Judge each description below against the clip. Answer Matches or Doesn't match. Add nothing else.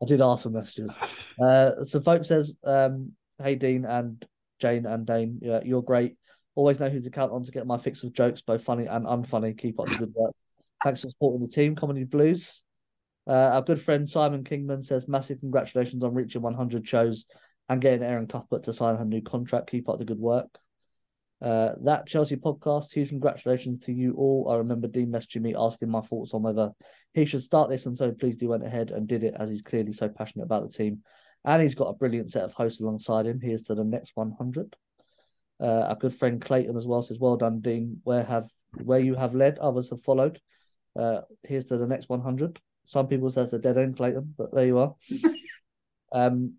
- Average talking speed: Doesn't match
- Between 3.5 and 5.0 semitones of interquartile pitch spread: Doesn't match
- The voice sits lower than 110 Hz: Doesn't match